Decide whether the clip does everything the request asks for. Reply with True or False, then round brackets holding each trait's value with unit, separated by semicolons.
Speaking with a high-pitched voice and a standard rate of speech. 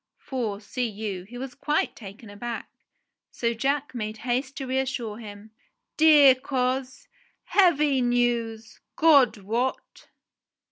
False (245 Hz; 120 wpm)